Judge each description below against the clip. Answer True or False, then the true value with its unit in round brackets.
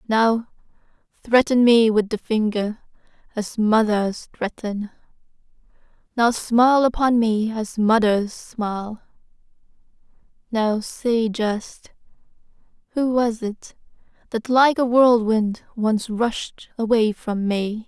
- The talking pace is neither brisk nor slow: False (105 wpm)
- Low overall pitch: False (225 Hz)